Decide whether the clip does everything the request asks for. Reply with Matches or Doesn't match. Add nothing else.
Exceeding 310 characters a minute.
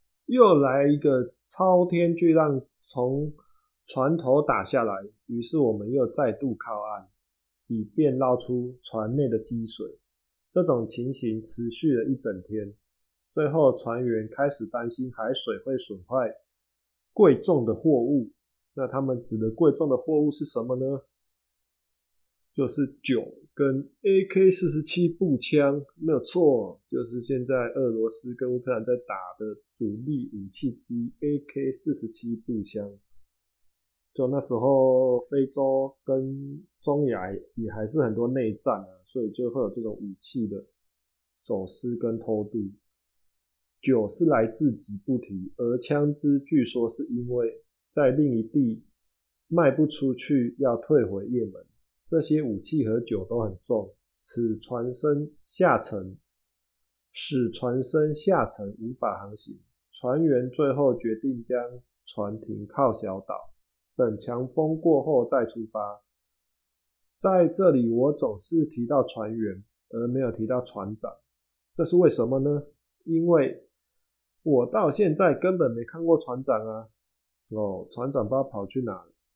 Doesn't match